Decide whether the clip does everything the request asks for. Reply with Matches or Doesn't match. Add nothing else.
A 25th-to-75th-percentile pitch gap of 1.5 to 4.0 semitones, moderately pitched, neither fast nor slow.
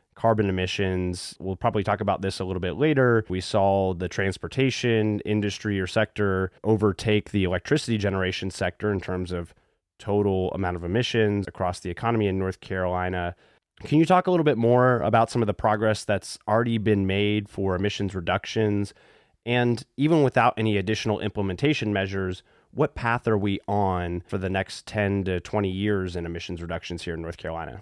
Doesn't match